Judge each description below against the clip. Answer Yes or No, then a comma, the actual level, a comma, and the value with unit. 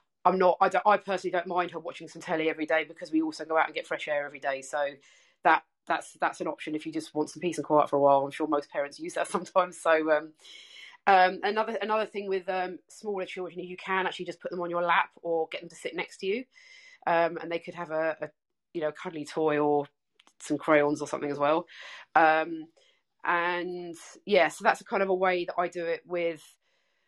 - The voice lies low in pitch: No, medium, 170 Hz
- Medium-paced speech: No, fast, 245 wpm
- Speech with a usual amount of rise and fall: Yes, average, 3.1 semitones